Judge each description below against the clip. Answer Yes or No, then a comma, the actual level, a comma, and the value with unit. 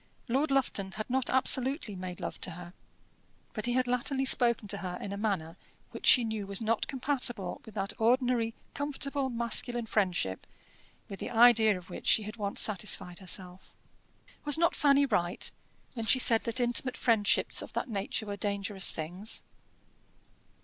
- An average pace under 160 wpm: No, average, 165 wpm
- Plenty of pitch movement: No, average, 4.2 semitones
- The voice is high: Yes, high, 220 Hz